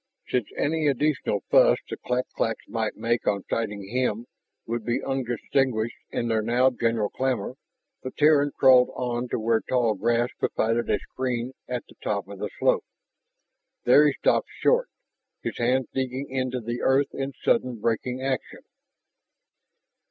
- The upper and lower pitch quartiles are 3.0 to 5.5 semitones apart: No, narrow, 2.4 semitones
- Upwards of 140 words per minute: Yes, average, 150 wpm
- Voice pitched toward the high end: No, low, 125 Hz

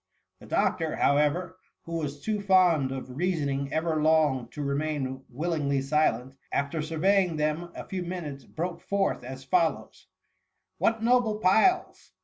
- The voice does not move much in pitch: No, average, 4.5 semitones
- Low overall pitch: No, medium, 155 Hz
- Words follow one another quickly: No, average, 145 wpm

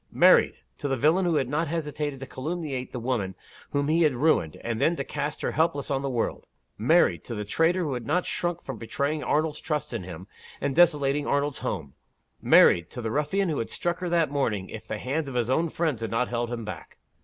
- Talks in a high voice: No, medium, 140 Hz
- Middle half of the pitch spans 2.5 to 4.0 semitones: No, average, 5.1 semitones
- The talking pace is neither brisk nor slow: No, fast, 230 wpm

